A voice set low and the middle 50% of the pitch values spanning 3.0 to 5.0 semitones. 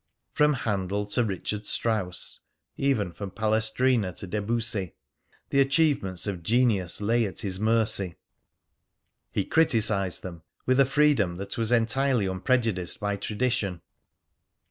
Yes: low, 110 Hz; average, 4.2 semitones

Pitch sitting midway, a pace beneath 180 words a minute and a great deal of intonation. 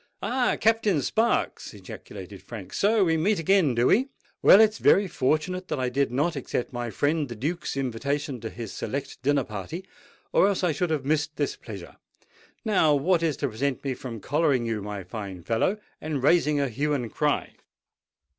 No: medium, 145 Hz; average, 185 wpm; wide, 6.2 semitones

